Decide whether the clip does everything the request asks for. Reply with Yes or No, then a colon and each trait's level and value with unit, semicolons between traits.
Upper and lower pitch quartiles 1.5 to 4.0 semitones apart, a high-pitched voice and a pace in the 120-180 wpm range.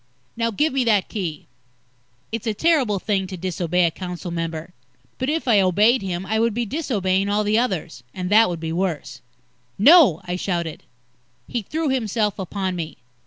No: average, 4.5 semitones; high, 200 Hz; average, 175 wpm